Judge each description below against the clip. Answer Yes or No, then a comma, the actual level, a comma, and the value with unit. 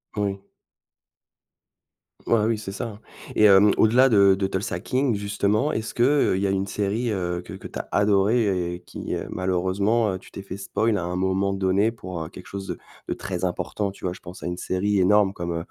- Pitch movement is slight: Yes, narrow, 2.3 semitones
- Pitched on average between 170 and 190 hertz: No, low, 100 Hz